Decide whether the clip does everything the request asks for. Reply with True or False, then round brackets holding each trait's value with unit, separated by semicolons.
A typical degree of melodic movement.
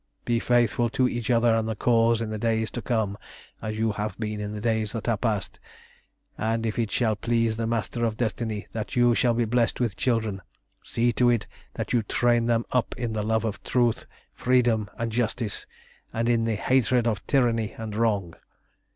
False (1.6 semitones)